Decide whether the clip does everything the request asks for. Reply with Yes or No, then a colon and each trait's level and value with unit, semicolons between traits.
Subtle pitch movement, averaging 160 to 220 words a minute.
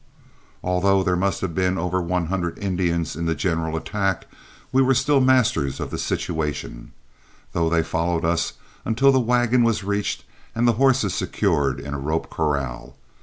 No: average, 5.2 semitones; average, 170 wpm